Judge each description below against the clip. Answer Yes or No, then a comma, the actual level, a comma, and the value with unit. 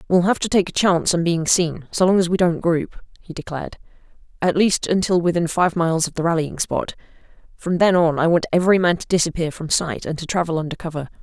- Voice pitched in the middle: Yes, medium, 170 Hz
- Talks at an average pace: No, fast, 230 wpm